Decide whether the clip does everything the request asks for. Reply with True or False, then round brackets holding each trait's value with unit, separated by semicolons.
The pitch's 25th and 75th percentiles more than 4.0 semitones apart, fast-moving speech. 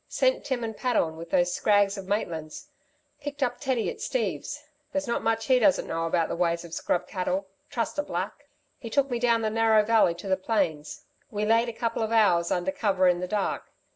True (4.9 semitones; 215 wpm)